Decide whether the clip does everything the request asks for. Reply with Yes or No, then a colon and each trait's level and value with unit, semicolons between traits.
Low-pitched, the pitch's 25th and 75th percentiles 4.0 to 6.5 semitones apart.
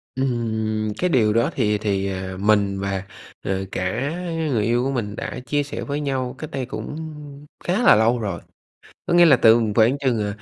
Yes: low, 115 Hz; average, 4.5 semitones